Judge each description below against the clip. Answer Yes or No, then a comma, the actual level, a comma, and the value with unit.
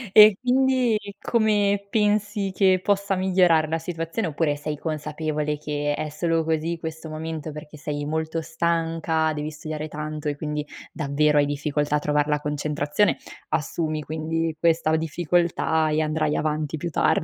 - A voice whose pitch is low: No, medium, 160 Hz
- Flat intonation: Yes, narrow, 2.2 semitones